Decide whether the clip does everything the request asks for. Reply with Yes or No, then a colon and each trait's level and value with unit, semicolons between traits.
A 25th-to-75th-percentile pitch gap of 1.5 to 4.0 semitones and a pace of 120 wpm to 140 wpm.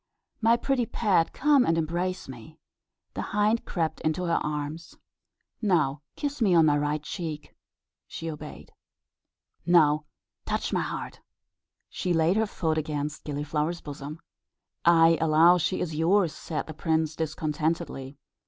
Yes: average, 2.9 semitones; slow, 135 wpm